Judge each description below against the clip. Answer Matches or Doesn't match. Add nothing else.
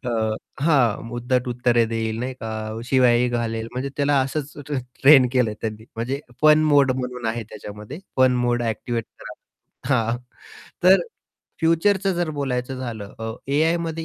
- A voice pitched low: Matches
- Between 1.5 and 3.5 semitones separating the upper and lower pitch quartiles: Doesn't match